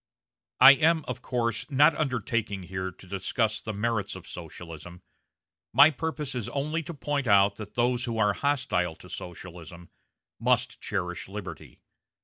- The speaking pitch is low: Yes, low, 110 Hz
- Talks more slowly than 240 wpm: Yes, average, 145 wpm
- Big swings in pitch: Yes, wide, 6.6 semitones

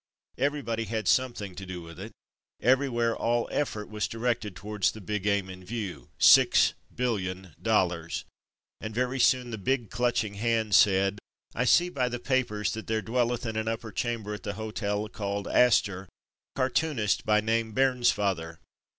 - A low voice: Yes, low, 110 Hz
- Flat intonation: No, average, 3.2 semitones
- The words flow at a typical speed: Yes, average, 165 wpm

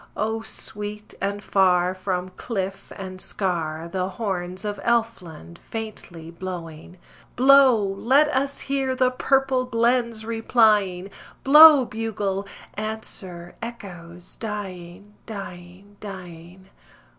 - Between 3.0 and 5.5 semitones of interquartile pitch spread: Yes, average, 4.2 semitones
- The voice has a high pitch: Yes, high, 200 Hz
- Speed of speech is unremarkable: No, slow, 100 wpm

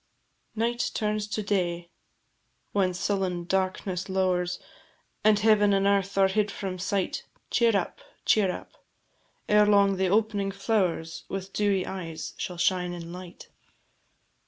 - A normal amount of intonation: No, narrow, 2.3 semitones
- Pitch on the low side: No, high, 195 Hz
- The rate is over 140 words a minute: No, slow, 135 wpm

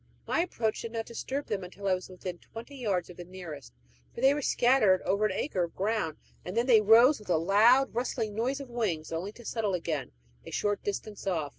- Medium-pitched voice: No, high, 210 Hz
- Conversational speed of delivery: No, fast, 225 wpm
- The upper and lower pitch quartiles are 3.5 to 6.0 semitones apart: Yes, average, 4.6 semitones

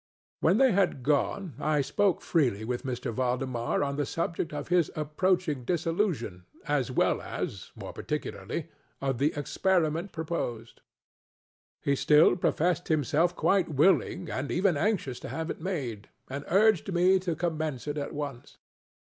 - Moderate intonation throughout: Yes, average, 4.6 semitones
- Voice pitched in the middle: Yes, medium, 155 Hz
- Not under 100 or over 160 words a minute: Yes, average, 150 wpm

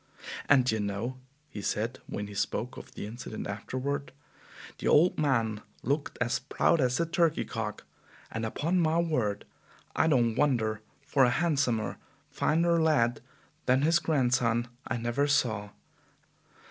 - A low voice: Yes, low, 125 Hz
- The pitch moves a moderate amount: Yes, average, 5.0 semitones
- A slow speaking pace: No, average, 145 wpm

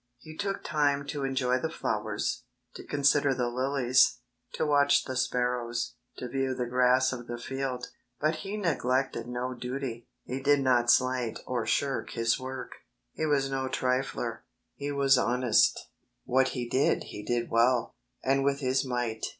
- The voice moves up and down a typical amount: No, narrow, 2.0 semitones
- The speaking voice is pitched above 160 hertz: No, low, 130 Hz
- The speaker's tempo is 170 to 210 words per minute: Yes, average, 175 wpm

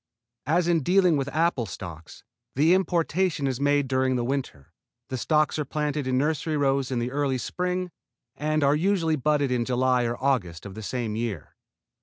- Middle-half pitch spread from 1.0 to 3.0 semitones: No, average, 3.8 semitones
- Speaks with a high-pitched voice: No, medium, 140 Hz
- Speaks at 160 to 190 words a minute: Yes, average, 180 wpm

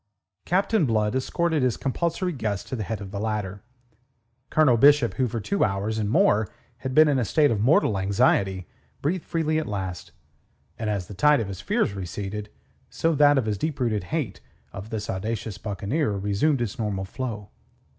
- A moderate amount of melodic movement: No, wide, 6.2 semitones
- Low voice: Yes, low, 110 Hz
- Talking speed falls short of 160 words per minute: No, average, 185 wpm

